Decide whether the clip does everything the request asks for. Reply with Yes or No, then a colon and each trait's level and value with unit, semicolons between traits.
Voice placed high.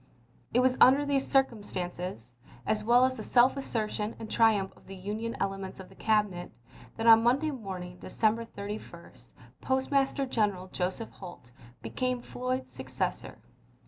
Yes: high, 220 Hz